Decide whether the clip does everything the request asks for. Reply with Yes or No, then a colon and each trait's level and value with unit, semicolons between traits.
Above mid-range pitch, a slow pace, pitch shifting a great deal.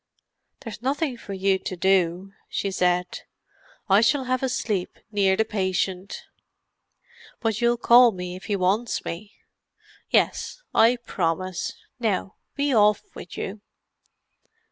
No: high, 200 Hz; slow, 125 wpm; average, 4.1 semitones